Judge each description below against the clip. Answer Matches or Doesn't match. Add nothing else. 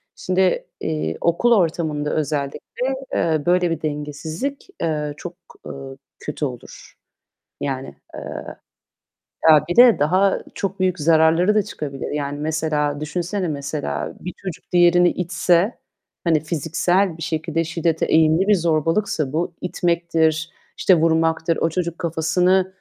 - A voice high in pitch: Doesn't match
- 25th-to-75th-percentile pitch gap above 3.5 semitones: Doesn't match